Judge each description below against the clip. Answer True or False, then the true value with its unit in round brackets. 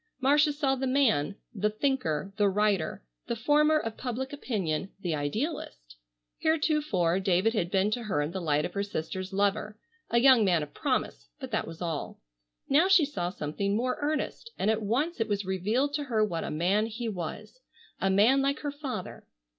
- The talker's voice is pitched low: False (215 Hz)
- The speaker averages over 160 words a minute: True (185 wpm)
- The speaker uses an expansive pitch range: True (6.5 semitones)